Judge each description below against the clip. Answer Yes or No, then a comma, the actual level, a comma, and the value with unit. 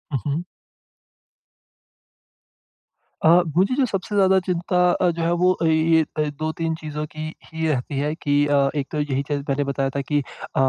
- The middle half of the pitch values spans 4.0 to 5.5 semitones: No, average, 3.2 semitones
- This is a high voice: No, medium, 155 Hz